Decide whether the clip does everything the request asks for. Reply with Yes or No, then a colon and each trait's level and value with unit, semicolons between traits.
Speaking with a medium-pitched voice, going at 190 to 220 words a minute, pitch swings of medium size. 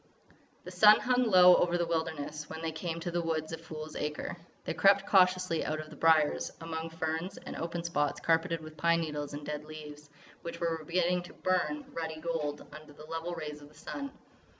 No: medium, 165 Hz; average, 200 wpm; narrow, 2.1 semitones